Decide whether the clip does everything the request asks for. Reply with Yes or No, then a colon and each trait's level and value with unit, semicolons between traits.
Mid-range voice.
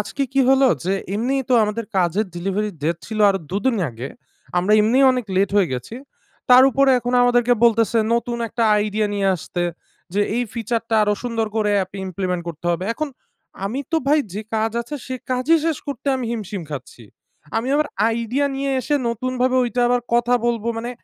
No: high, 230 Hz